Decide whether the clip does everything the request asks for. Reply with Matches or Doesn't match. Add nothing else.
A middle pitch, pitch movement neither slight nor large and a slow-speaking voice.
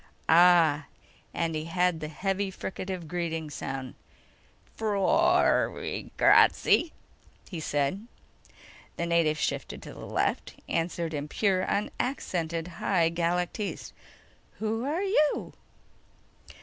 Matches